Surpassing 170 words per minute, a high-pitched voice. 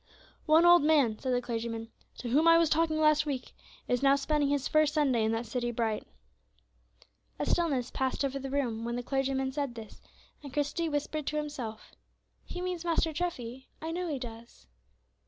Yes: average, 185 wpm; very high, 275 Hz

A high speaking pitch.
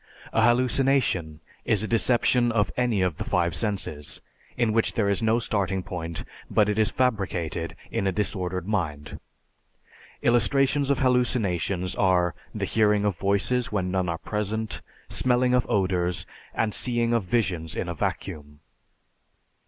No: low, 105 Hz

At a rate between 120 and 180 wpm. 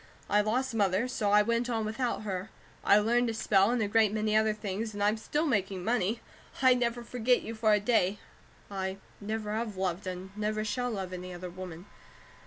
No: average, 200 wpm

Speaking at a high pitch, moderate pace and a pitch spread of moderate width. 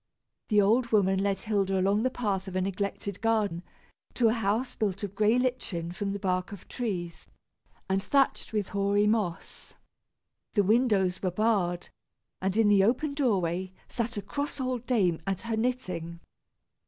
Yes: high, 205 Hz; average, 165 wpm; average, 3.3 semitones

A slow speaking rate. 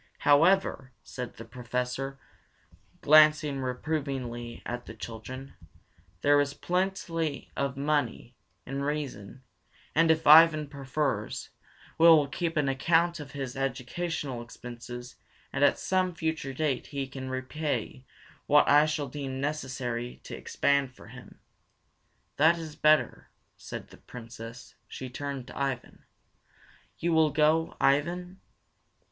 Yes: slow, 125 wpm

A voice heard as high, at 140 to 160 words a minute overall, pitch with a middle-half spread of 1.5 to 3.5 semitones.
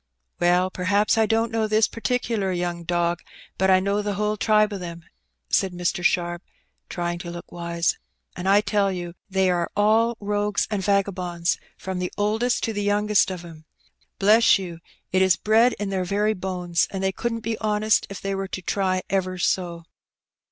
No: high, 195 Hz; average, 190 wpm; average, 3.0 semitones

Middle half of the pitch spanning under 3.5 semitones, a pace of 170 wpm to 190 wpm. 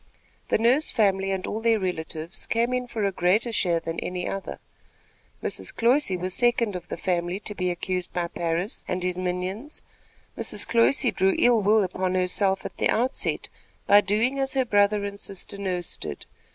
No: average, 3.9 semitones; average, 180 wpm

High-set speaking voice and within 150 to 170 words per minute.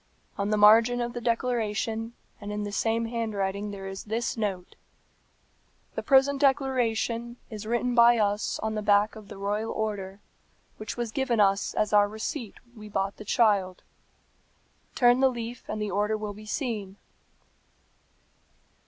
Yes: high, 220 Hz; average, 160 wpm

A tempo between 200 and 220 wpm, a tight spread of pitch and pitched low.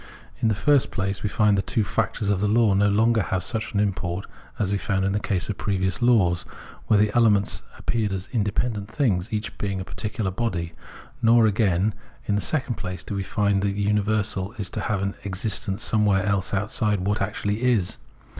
Yes: fast, 205 wpm; narrow, 2.1 semitones; low, 105 Hz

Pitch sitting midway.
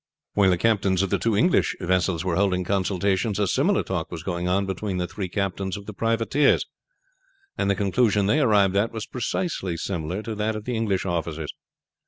No: low, 100 Hz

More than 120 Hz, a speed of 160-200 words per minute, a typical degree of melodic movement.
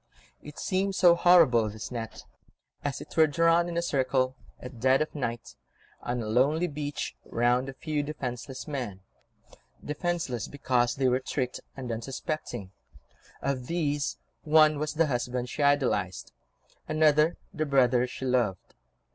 No: low, 135 Hz; average, 145 wpm; average, 3.8 semitones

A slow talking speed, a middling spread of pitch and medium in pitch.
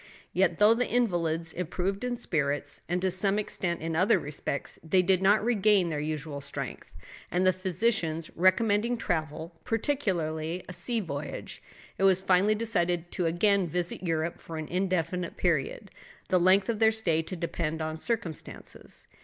No: average, 160 wpm; average, 3.7 semitones; medium, 180 Hz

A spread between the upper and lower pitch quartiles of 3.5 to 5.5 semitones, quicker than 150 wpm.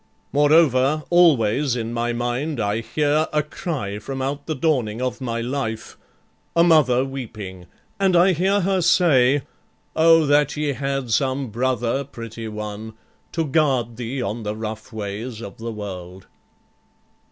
No: average, 5.0 semitones; average, 145 wpm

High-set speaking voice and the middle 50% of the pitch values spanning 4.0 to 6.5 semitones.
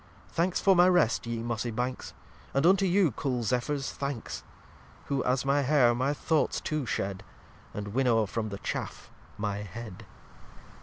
No: low, 125 Hz; average, 4.7 semitones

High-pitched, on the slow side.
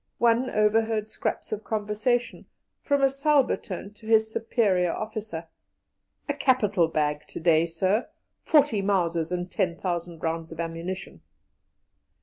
Yes: high, 205 Hz; slow, 130 wpm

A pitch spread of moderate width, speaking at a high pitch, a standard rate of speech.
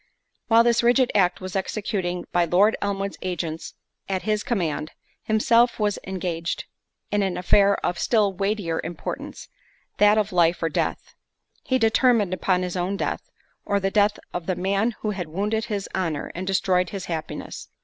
Yes: average, 3.0 semitones; high, 195 Hz; average, 160 wpm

